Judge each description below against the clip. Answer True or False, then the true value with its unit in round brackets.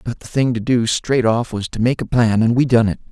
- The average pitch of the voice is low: True (115 Hz)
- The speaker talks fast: True (310 wpm)